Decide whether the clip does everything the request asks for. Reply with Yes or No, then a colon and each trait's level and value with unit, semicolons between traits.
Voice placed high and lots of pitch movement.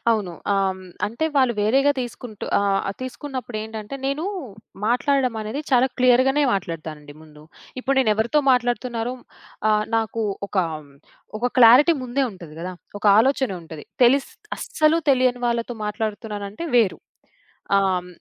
No: high, 235 Hz; average, 4.0 semitones